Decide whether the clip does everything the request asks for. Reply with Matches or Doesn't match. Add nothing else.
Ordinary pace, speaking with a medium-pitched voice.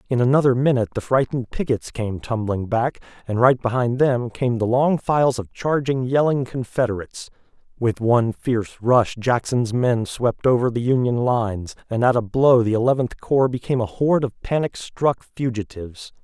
Doesn't match